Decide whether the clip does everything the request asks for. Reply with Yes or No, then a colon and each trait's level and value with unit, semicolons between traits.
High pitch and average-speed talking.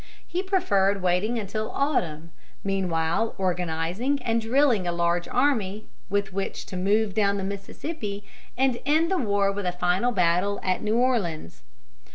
Yes: high, 200 Hz; average, 150 wpm